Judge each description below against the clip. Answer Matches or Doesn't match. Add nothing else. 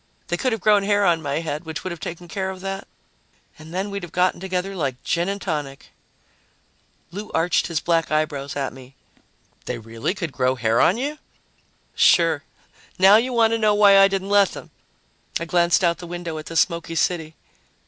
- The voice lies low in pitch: Doesn't match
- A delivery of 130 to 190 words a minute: Doesn't match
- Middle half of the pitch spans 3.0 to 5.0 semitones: Matches